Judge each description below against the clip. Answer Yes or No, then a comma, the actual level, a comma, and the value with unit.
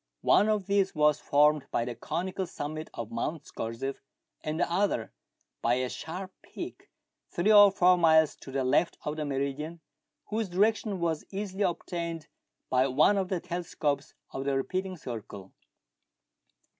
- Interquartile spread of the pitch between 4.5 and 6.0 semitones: Yes, wide, 5.4 semitones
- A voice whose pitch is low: No, medium, 160 Hz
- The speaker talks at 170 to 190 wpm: No, average, 155 wpm